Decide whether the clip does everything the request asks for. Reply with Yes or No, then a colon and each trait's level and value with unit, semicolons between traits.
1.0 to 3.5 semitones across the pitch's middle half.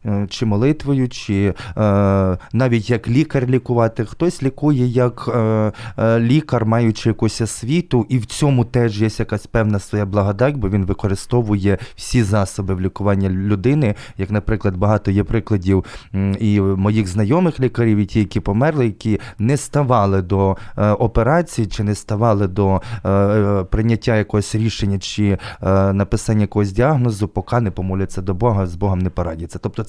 Yes: average, 3.2 semitones